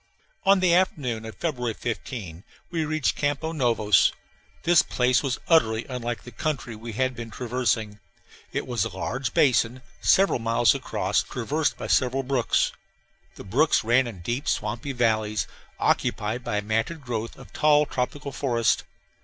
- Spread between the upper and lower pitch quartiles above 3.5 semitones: Yes, average, 4.0 semitones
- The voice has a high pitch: No, low, 125 Hz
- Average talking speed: Yes, average, 155 wpm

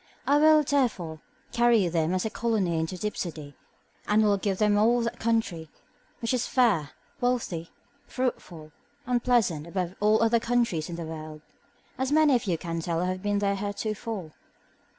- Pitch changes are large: Yes, wide, 5.8 semitones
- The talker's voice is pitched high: Yes, high, 205 Hz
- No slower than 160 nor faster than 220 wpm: Yes, average, 170 wpm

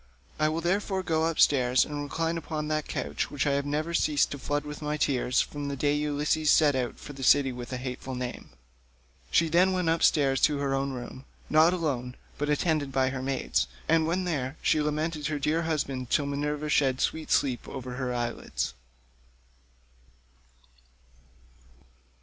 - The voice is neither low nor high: Yes, medium, 145 Hz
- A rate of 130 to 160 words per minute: No, average, 175 wpm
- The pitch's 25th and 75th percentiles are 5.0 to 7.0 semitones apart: No, average, 2.7 semitones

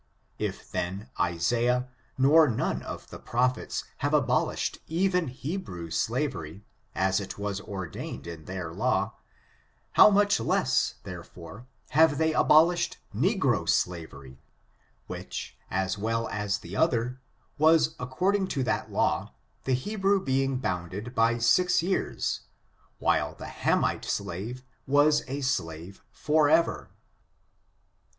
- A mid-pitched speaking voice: No, low, 125 Hz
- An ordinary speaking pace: No, slow, 120 wpm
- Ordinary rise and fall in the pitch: No, wide, 8.3 semitones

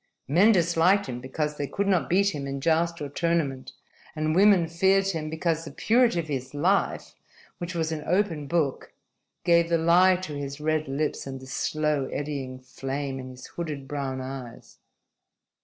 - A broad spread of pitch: No, average, 3.8 semitones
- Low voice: No, medium, 155 Hz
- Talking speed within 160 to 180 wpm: Yes, average, 175 wpm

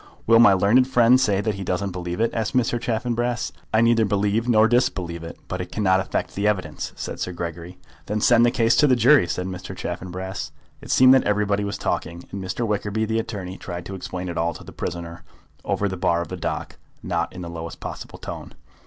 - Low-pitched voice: Yes, low, 100 Hz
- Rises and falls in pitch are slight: No, average, 4.1 semitones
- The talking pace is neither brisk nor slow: No, fast, 220 wpm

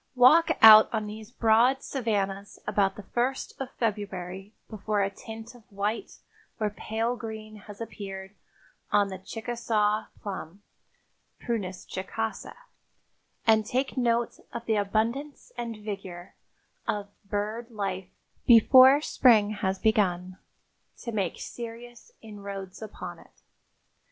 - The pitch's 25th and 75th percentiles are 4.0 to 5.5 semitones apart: No, average, 2.8 semitones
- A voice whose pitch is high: Yes, high, 215 Hz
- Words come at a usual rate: No, slow, 120 wpm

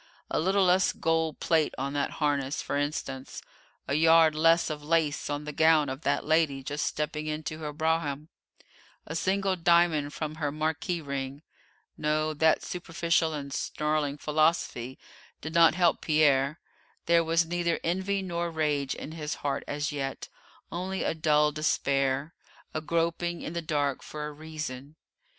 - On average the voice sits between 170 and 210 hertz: No, medium, 155 Hz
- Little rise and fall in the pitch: Yes, narrow, 2.2 semitones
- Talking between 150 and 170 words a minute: Yes, average, 155 wpm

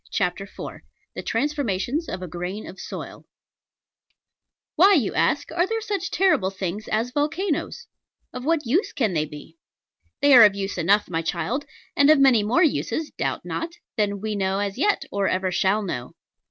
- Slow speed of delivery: No, average, 175 wpm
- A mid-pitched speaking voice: No, high, 220 Hz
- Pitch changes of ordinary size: No, wide, 7.8 semitones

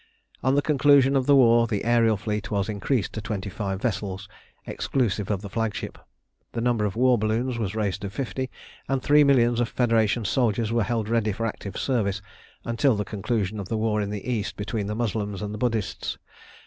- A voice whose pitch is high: No, low, 110 Hz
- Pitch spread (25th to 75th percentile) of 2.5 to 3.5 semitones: Yes, average, 2.8 semitones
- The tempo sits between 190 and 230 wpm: Yes, average, 195 wpm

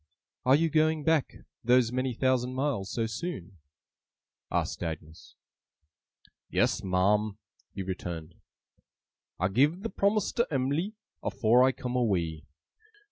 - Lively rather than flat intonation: Yes, wide, 7.4 semitones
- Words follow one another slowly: Yes, slow, 120 wpm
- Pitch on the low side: Yes, low, 125 Hz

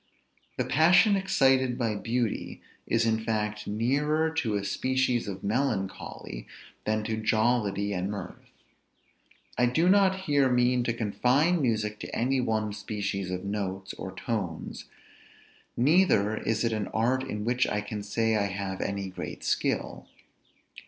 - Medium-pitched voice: No, low, 110 Hz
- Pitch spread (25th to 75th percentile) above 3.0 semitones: Yes, average, 4.1 semitones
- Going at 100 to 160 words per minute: Yes, average, 145 wpm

